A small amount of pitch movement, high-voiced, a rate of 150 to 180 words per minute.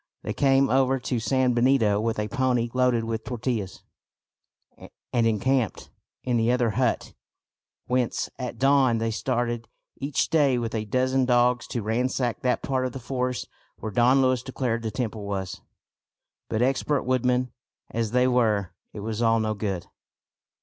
No: narrow, 2.3 semitones; low, 120 Hz; average, 155 wpm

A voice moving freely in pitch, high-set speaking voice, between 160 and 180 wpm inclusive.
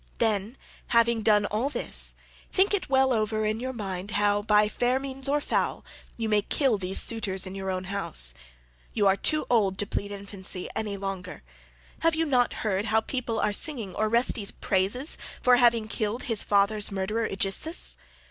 No: average, 3.6 semitones; high, 215 Hz; average, 175 wpm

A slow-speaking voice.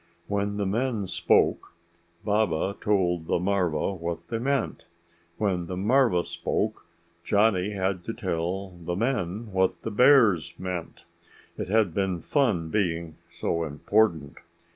Yes: slow, 130 wpm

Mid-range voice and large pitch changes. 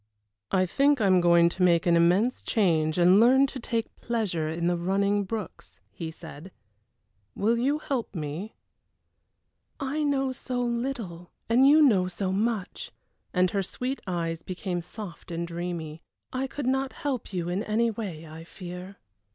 No: high, 195 Hz; wide, 5.7 semitones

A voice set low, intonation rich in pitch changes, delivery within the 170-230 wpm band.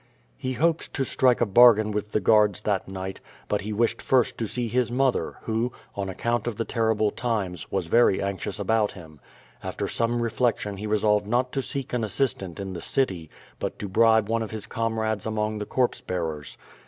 No: low, 110 Hz; average, 3.0 semitones; average, 200 wpm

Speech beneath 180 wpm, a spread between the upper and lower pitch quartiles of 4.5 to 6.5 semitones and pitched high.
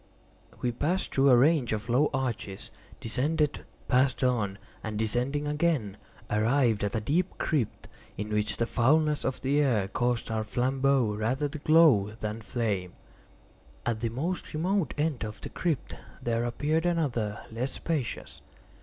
No: average, 150 wpm; average, 5.1 semitones; low, 125 Hz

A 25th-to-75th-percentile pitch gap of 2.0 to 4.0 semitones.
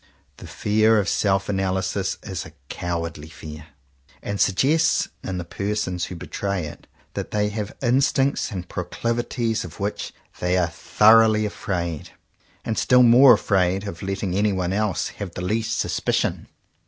Yes: average, 3.3 semitones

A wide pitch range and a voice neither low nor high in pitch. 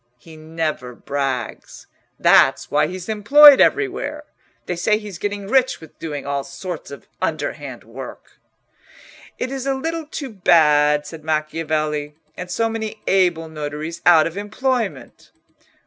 Yes: wide, 6.5 semitones; medium, 170 Hz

